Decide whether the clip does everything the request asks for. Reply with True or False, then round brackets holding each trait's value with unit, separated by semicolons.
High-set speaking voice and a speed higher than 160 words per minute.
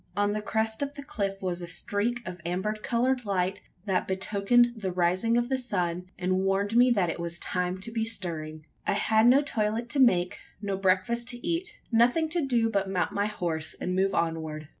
True (205 Hz; 205 wpm)